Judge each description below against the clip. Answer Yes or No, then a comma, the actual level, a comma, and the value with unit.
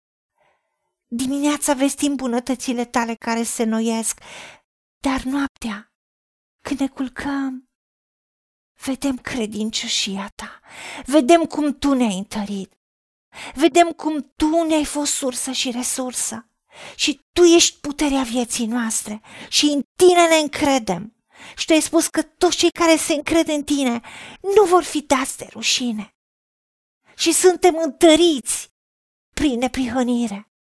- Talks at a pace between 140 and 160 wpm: No, average, 120 wpm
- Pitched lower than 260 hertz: No, very high, 275 Hz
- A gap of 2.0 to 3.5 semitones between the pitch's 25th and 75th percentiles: No, average, 4.3 semitones